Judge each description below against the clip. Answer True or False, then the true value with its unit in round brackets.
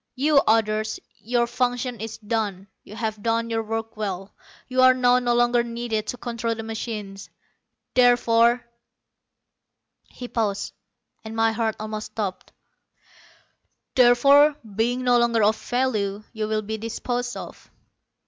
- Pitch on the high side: True (230 Hz)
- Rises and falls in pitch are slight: True (2.1 semitones)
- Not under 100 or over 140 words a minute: True (135 wpm)